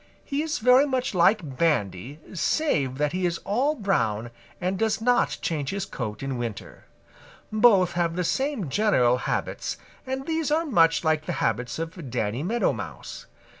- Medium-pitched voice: Yes, medium, 175 Hz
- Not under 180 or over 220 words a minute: No, average, 165 wpm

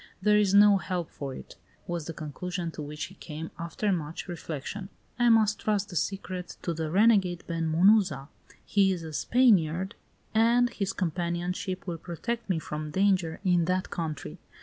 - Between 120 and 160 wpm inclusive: No, average, 170 wpm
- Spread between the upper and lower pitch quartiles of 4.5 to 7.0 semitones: No, average, 3.7 semitones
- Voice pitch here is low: No, medium, 180 Hz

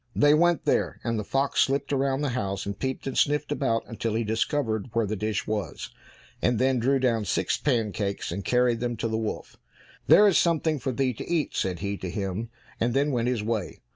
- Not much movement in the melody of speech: No, average, 4.1 semitones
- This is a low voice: Yes, low, 120 Hz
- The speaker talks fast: Yes, fast, 215 wpm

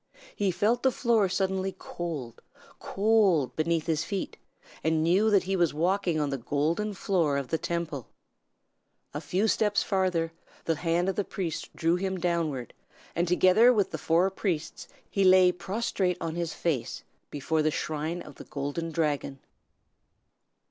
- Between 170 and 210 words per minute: No, average, 155 wpm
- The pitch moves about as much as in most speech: Yes, average, 3.5 semitones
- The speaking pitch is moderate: Yes, medium, 175 Hz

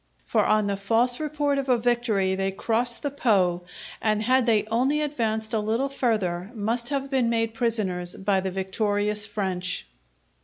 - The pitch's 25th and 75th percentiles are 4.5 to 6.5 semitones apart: No, average, 3.8 semitones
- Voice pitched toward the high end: Yes, high, 220 Hz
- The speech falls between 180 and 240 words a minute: No, average, 165 wpm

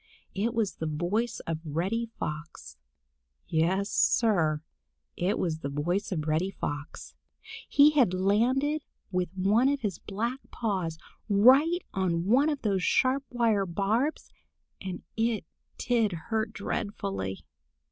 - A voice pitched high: Yes, high, 200 Hz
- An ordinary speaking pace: No, slow, 125 wpm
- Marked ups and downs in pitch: Yes, wide, 5.7 semitones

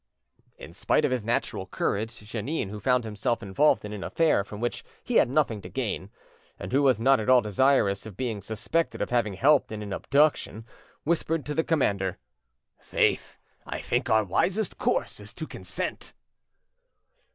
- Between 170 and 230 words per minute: Yes, average, 175 wpm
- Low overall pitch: Yes, low, 115 Hz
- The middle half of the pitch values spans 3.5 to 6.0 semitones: Yes, average, 5.0 semitones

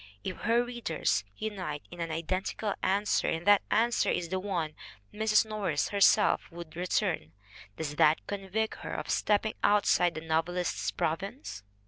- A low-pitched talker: No, medium, 185 Hz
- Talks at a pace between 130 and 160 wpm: Yes, average, 145 wpm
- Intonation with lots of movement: No, average, 4.3 semitones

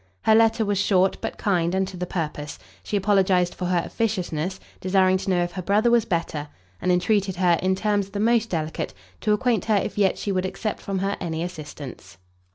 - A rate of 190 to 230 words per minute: Yes, fast, 205 wpm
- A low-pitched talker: No, high, 190 Hz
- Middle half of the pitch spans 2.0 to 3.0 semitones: Yes, average, 2.7 semitones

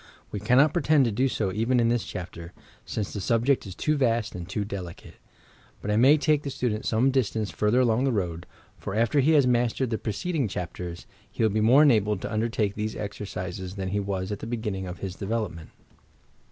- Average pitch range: Yes, average, 4.3 semitones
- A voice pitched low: Yes, low, 110 Hz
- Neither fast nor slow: No, fast, 220 wpm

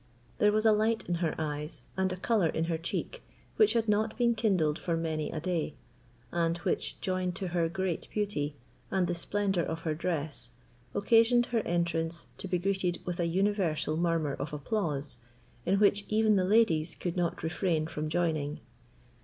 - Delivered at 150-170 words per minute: No, average, 180 wpm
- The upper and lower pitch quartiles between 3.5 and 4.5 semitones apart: Yes, average, 4.0 semitones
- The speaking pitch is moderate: Yes, medium, 175 Hz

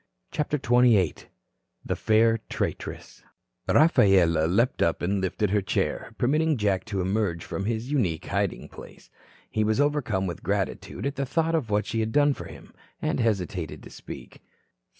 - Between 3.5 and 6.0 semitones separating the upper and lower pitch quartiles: Yes, wide, 5.5 semitones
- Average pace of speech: Yes, average, 160 wpm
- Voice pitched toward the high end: No, low, 110 Hz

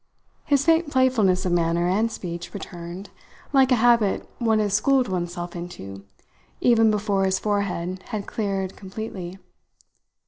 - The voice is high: Yes, high, 195 Hz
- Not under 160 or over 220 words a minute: No, slow, 135 wpm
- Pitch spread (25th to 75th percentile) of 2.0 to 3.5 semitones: No, average, 4.2 semitones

